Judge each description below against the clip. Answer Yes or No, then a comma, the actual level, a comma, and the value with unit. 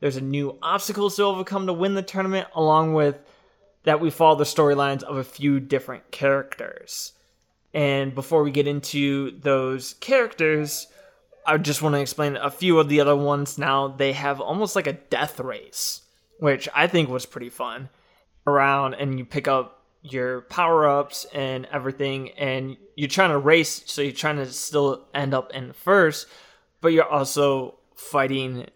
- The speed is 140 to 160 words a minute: No, average, 170 wpm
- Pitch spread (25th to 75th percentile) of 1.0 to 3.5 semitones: Yes, average, 2.8 semitones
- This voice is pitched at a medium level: Yes, medium, 145 Hz